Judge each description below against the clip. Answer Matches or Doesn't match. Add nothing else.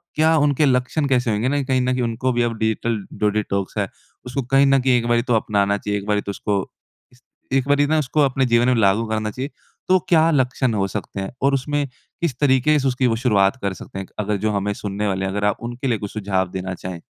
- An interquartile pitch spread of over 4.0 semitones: Matches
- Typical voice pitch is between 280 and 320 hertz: Doesn't match